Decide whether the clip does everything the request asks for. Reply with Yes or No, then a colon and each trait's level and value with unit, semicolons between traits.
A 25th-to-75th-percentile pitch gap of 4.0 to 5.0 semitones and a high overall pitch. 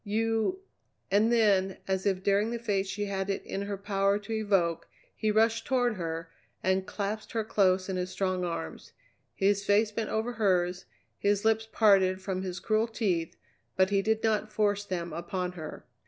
No: narrow, 2.5 semitones; high, 200 Hz